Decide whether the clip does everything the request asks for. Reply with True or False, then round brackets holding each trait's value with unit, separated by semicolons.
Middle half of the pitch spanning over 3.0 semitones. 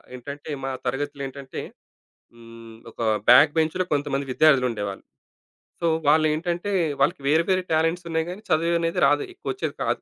True (4.0 semitones)